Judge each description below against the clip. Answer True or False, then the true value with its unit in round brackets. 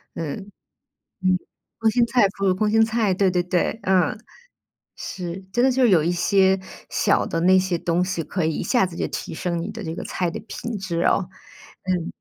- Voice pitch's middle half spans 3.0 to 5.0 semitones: True (3.5 semitones)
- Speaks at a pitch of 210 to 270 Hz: False (185 Hz)